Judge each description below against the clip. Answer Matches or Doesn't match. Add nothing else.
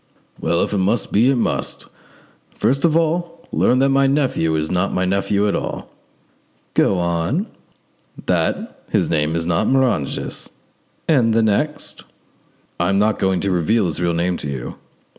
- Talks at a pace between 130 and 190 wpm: Matches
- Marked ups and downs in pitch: Matches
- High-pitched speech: Doesn't match